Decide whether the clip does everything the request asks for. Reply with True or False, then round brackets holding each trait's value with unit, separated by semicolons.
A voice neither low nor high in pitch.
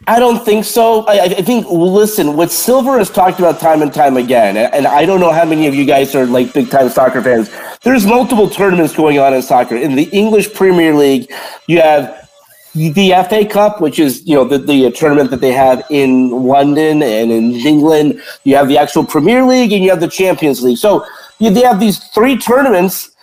True (165 Hz)